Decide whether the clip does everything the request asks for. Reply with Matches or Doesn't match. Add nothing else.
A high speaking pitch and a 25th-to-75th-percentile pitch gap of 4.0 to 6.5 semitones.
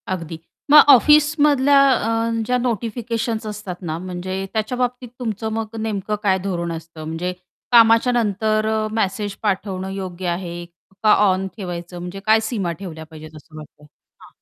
Matches